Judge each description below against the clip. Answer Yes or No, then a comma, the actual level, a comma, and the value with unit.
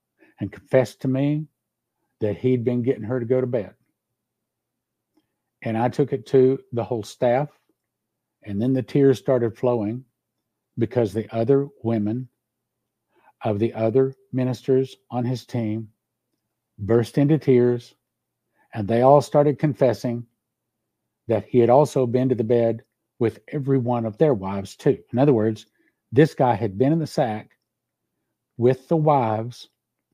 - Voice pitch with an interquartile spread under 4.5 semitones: Yes, average, 2.7 semitones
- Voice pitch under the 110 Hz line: No, low, 120 Hz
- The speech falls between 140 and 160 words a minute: Yes, average, 145 wpm